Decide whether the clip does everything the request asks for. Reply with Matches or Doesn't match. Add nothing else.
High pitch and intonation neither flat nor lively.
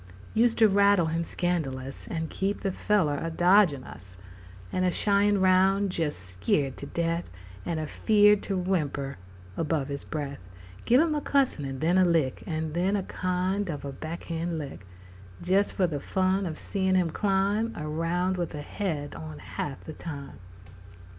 Doesn't match